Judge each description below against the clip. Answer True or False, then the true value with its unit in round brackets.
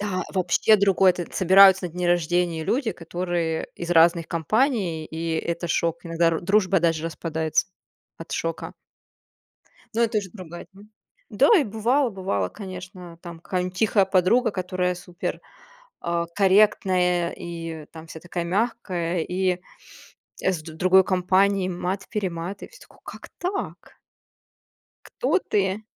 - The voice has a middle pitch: True (180 Hz)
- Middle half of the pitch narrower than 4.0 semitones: True (2.6 semitones)